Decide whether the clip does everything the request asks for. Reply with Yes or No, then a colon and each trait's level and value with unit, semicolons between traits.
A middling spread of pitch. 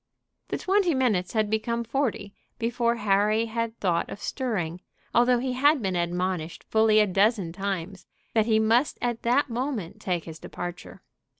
Yes: average, 4.3 semitones